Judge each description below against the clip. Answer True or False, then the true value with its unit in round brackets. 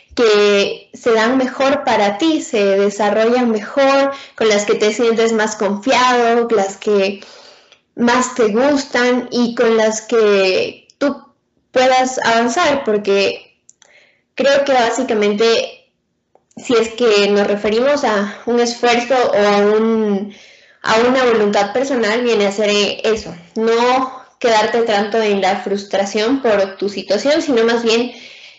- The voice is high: True (230 Hz)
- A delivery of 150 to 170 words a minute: False (135 wpm)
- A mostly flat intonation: False (3.5 semitones)